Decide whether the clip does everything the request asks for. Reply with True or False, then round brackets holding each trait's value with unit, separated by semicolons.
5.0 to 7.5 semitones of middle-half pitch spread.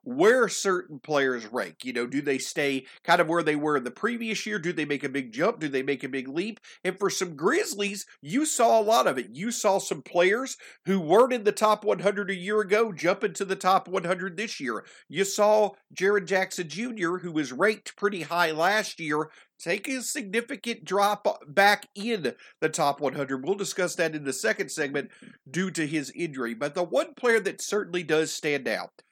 True (5.4 semitones)